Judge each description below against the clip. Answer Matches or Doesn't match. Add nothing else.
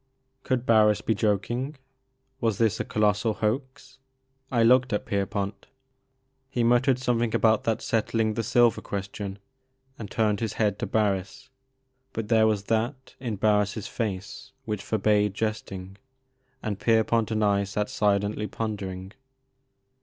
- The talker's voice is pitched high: Doesn't match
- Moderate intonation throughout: Doesn't match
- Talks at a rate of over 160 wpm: Doesn't match